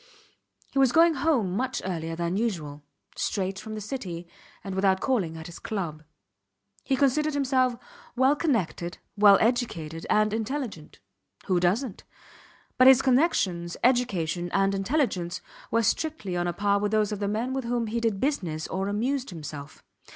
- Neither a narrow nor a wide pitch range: No, wide, 6.4 semitones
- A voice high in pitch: Yes, high, 210 Hz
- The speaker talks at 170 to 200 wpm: No, average, 160 wpm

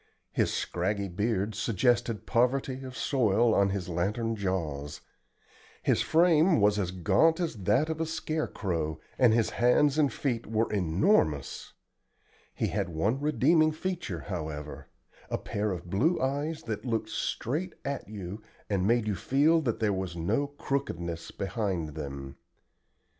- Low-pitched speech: Yes, low, 110 Hz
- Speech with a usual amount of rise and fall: No, wide, 7.1 semitones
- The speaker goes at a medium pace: Yes, average, 145 wpm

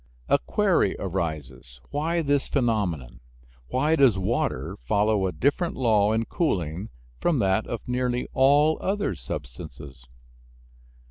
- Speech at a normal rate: No, slow, 120 wpm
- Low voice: Yes, low, 110 Hz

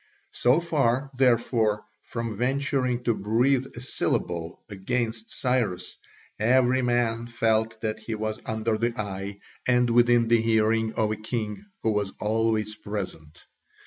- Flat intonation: Yes, narrow, 2.3 semitones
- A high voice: No, low, 115 Hz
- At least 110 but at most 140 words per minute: Yes, slow, 135 wpm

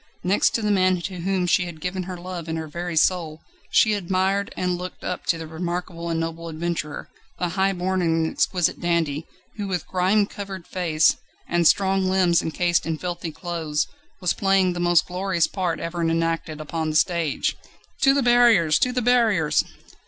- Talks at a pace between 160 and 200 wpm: Yes, average, 180 wpm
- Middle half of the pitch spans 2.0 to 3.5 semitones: Yes, narrow, 2.4 semitones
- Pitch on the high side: No, medium, 175 Hz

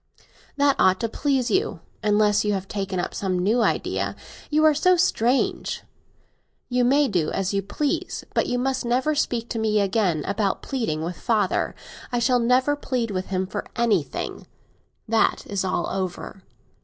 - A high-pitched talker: Yes, high, 220 Hz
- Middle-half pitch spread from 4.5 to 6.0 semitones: Yes, average, 4.8 semitones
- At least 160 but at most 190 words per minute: Yes, average, 165 wpm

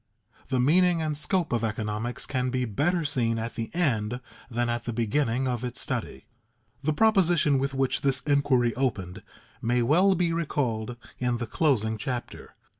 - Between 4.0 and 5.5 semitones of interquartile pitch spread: Yes, average, 4.3 semitones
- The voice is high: No, low, 125 Hz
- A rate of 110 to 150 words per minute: No, average, 165 wpm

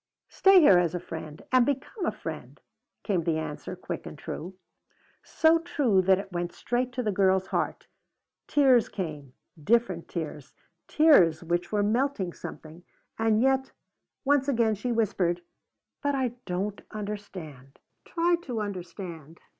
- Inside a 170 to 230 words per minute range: No, average, 145 wpm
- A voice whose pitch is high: Yes, high, 200 Hz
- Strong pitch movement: Yes, wide, 6.7 semitones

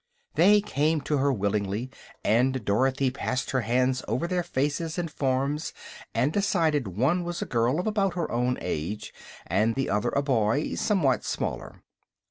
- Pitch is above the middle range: No, low, 135 Hz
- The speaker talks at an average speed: Yes, average, 160 wpm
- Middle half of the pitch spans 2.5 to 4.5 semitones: No, average, 5.3 semitones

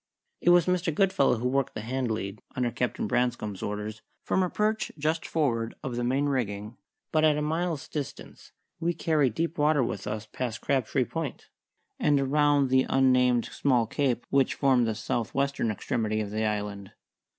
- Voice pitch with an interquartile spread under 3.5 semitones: No, average, 4.9 semitones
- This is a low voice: Yes, low, 130 Hz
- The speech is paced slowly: No, average, 175 wpm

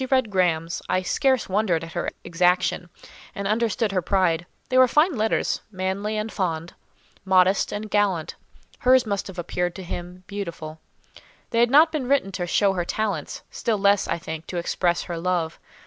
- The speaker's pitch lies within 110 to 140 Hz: No, high, 190 Hz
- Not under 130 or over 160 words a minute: No, average, 175 wpm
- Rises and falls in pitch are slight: No, average, 3.6 semitones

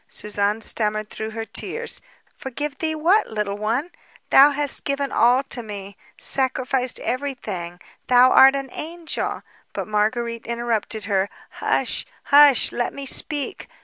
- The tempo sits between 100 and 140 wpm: Yes, slow, 135 wpm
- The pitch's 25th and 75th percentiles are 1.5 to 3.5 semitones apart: No, average, 4.6 semitones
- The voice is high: Yes, high, 245 Hz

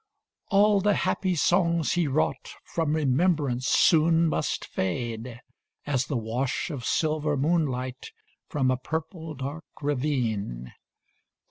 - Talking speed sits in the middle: No, slow, 120 wpm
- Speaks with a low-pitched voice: No, medium, 145 Hz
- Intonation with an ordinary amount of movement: Yes, average, 4.4 semitones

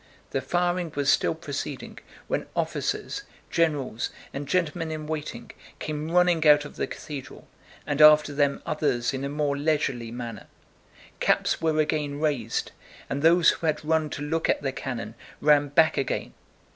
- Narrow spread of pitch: Yes, narrow, 2.3 semitones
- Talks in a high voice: No, medium, 150 Hz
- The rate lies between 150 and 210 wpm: Yes, average, 160 wpm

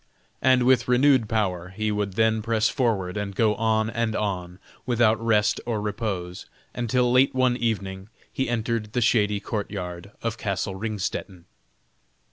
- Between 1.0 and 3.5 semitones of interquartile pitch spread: Yes, average, 2.9 semitones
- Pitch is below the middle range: Yes, low, 110 Hz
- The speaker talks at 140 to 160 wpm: Yes, average, 150 wpm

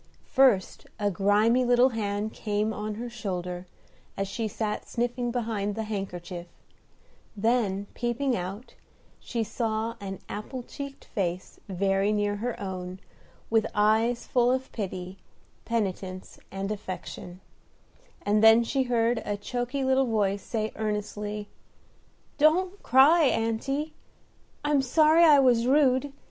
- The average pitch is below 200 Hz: No, high, 220 Hz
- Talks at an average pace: No, slow, 125 wpm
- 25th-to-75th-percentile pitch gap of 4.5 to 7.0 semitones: No, average, 3.6 semitones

